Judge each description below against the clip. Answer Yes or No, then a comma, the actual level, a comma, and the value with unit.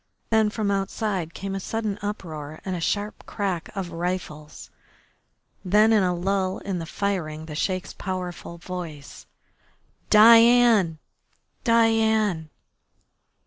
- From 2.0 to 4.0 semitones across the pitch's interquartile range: Yes, average, 3.7 semitones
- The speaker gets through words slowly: Yes, slow, 115 wpm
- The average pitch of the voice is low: No, high, 190 Hz